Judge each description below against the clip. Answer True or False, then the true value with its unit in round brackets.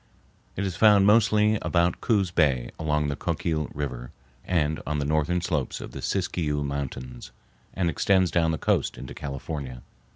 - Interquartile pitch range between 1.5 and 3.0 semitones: False (4.5 semitones)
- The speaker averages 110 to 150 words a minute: False (160 wpm)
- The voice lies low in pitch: True (80 Hz)